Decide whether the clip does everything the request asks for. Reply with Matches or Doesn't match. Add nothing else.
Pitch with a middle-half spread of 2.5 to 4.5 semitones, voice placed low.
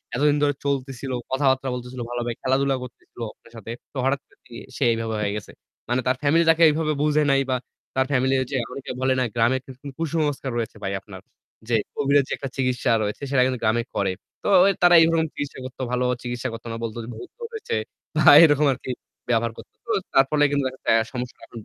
Matches